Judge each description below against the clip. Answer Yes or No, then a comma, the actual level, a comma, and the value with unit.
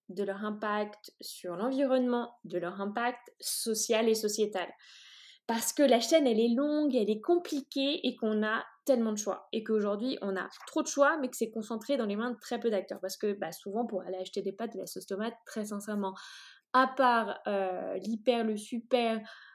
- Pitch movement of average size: Yes, average, 3.6 semitones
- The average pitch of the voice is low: No, high, 225 Hz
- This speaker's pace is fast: No, average, 205 wpm